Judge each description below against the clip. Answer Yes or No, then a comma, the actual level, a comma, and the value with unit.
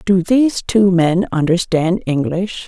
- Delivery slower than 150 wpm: Yes, slow, 135 wpm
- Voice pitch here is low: No, medium, 185 Hz